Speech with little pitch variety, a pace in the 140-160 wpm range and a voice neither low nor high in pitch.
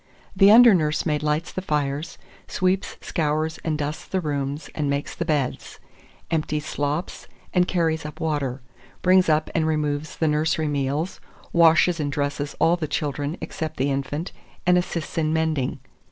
Yes: narrow, 2.3 semitones; average, 155 wpm; medium, 155 Hz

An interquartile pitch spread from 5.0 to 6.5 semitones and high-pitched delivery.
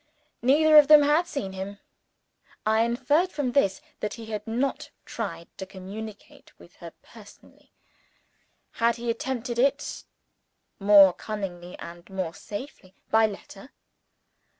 Yes: average, 5.3 semitones; high, 220 Hz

